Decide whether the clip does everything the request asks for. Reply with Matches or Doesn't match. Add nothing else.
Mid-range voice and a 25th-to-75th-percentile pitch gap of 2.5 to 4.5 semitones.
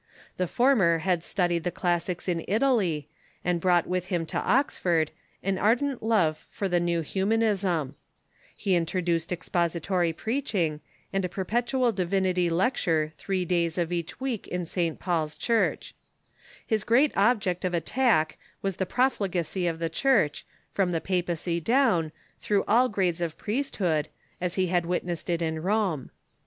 Matches